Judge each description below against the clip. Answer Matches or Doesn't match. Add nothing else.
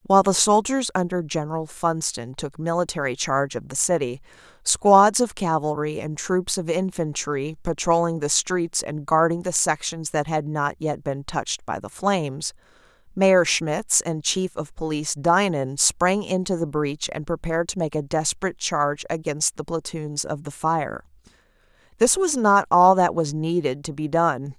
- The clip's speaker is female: Matches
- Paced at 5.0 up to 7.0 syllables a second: Doesn't match